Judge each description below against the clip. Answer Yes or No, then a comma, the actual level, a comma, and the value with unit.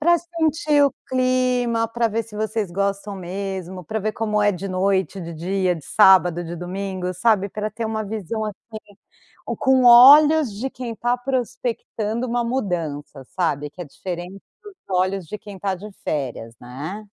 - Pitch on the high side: Yes, high, 205 Hz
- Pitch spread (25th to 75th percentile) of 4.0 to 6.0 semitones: Yes, average, 4.5 semitones